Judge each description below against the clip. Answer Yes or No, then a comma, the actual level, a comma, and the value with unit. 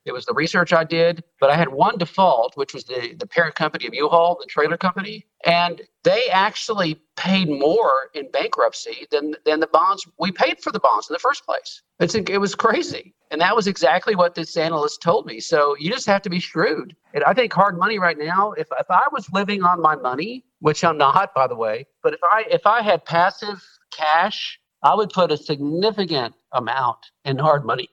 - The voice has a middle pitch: Yes, medium, 175 Hz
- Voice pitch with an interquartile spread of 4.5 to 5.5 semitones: Yes, average, 4.9 semitones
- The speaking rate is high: Yes, fast, 215 wpm